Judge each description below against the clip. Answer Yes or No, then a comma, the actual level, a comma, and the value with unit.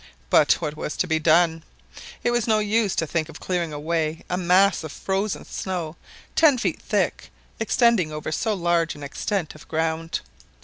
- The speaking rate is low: No, average, 175 wpm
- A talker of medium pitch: Yes, medium, 170 Hz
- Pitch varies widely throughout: No, average, 4.0 semitones